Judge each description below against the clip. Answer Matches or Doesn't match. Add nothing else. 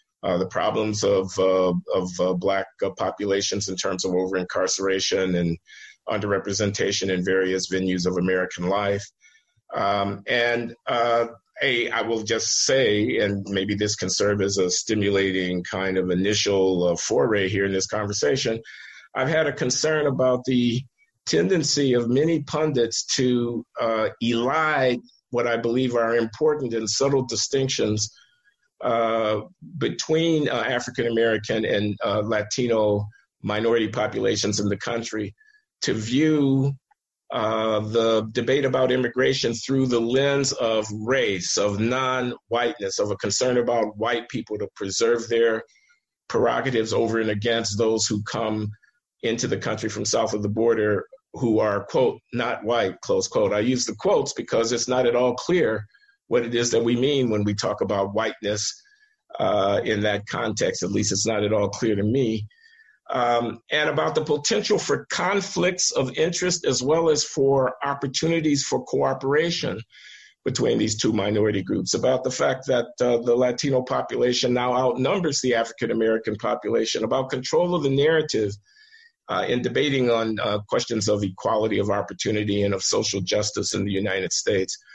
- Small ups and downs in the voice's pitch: Doesn't match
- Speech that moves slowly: Doesn't match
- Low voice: Matches